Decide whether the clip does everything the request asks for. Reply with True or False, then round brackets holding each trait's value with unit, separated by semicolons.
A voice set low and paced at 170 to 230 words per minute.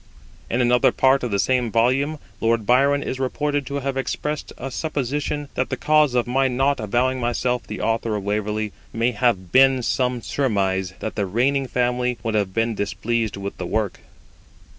True (125 Hz; 180 wpm)